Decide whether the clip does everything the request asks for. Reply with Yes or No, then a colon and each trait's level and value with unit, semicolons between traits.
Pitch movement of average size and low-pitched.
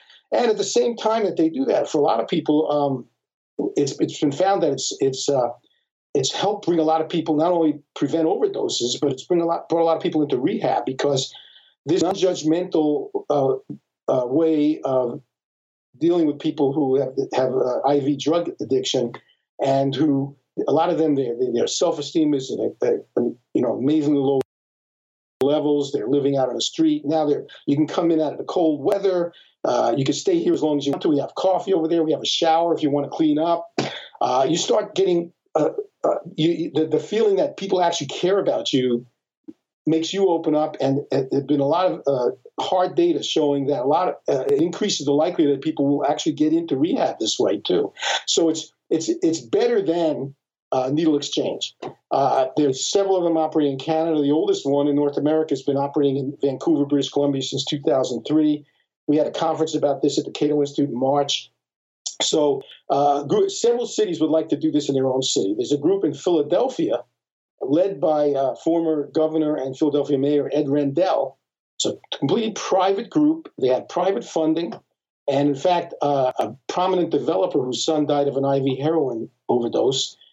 No: average, 4.3 semitones; medium, 155 Hz